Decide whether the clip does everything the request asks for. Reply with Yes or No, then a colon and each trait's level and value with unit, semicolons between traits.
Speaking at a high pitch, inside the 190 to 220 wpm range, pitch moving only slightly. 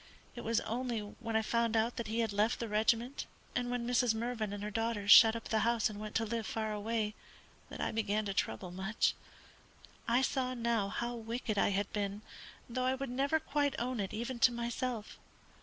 Yes: high, 230 Hz; fast, 205 wpm; narrow, 2.2 semitones